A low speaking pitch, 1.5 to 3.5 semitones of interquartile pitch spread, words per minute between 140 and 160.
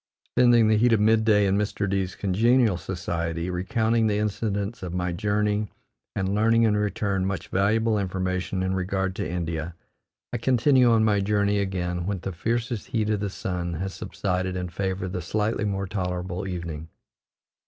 No: low, 100 Hz; average, 2.8 semitones; average, 175 wpm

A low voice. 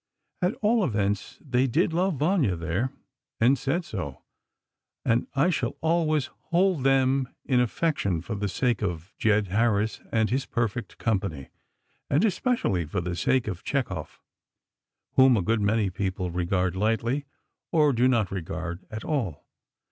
Yes: low, 115 Hz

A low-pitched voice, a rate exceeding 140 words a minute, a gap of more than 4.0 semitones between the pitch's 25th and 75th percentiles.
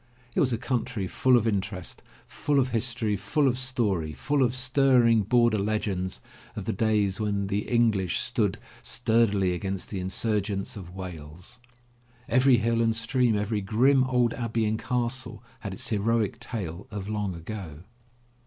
No: low, 110 Hz; average, 160 wpm; average, 3.7 semitones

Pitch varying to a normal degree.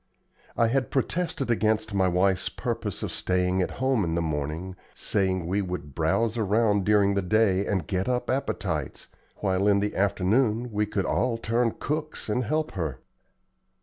Yes: average, 3.9 semitones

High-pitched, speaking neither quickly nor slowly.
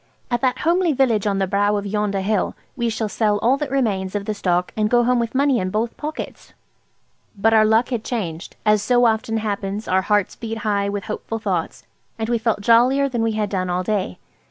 No: high, 215 Hz; fast, 220 wpm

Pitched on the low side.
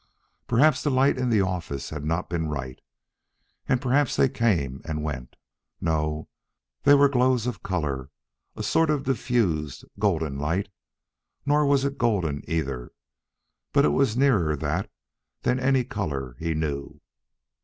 Yes: very low, 90 Hz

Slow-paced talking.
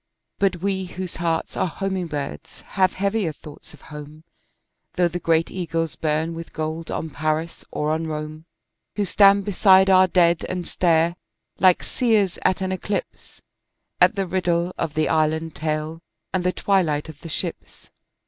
No: average, 160 wpm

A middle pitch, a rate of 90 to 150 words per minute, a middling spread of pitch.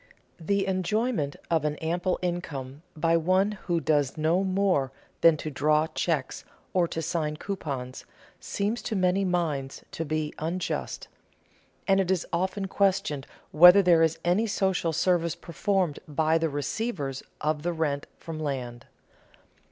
Yes: medium, 165 Hz; average, 145 wpm; average, 3.6 semitones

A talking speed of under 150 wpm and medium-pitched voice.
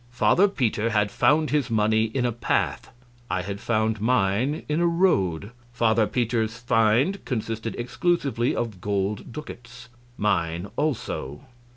No: average, 140 wpm; low, 115 Hz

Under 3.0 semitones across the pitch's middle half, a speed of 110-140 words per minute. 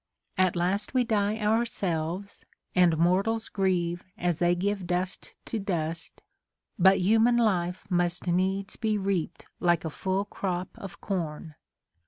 Yes: narrow, 2.6 semitones; slow, 135 wpm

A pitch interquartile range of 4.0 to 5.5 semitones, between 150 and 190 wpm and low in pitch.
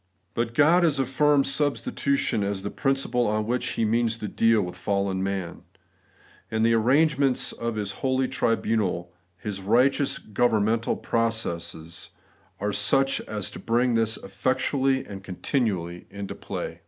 No: average, 4.7 semitones; average, 140 wpm; low, 115 Hz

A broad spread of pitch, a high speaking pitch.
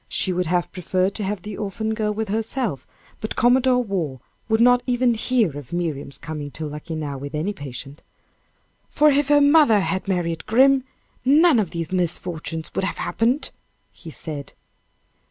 Yes: wide, 7.0 semitones; high, 195 Hz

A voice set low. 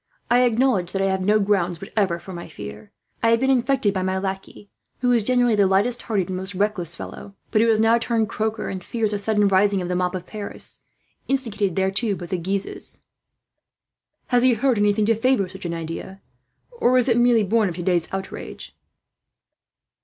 No: high, 205 Hz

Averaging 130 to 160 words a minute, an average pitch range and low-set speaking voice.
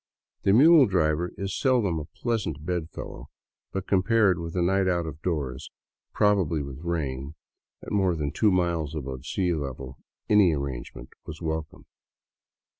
Yes: average, 150 wpm; average, 4.3 semitones; very low, 85 Hz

